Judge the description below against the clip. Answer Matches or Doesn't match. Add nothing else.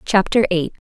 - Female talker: Matches